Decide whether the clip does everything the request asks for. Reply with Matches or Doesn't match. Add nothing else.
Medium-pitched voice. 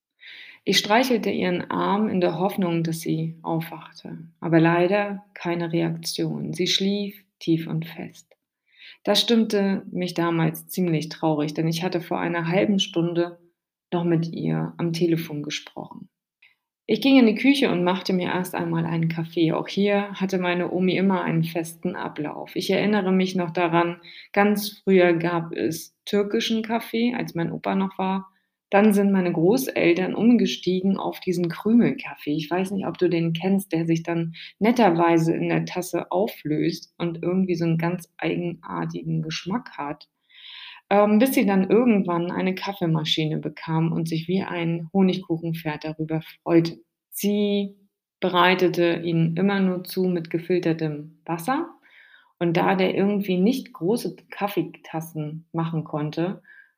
Matches